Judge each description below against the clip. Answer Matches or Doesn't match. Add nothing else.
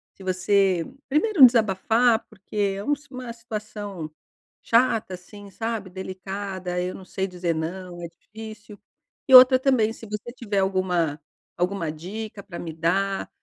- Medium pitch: Doesn't match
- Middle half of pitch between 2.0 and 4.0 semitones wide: Matches